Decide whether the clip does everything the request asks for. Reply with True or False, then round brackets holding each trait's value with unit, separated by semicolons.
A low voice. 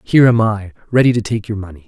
True (110 Hz)